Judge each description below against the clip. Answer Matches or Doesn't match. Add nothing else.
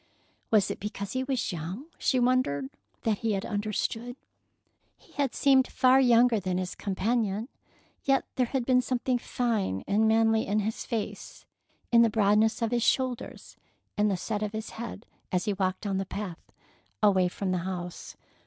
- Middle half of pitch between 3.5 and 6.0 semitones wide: Matches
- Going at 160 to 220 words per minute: Matches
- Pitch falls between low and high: Doesn't match